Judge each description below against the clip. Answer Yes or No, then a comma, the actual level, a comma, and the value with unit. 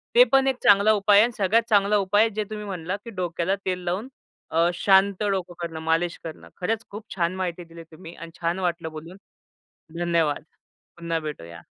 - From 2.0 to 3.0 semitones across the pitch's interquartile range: No, average, 3.4 semitones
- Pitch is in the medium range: Yes, medium, 180 Hz